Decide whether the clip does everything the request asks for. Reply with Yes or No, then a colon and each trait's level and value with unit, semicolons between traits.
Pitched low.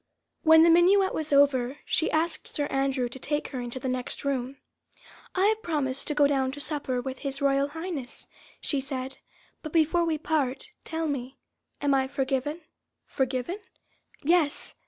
No: very high, 280 Hz